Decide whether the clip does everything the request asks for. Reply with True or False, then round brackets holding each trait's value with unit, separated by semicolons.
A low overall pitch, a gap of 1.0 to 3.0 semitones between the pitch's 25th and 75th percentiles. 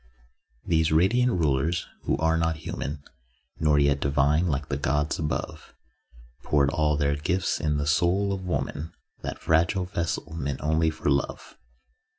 True (80 Hz; 2.7 semitones)